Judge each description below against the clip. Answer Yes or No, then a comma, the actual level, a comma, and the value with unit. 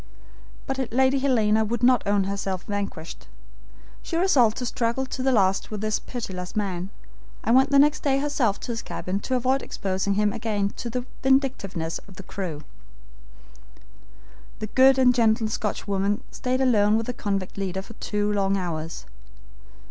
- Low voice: No, high, 215 Hz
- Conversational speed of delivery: Yes, average, 160 wpm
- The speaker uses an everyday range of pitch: Yes, average, 4.5 semitones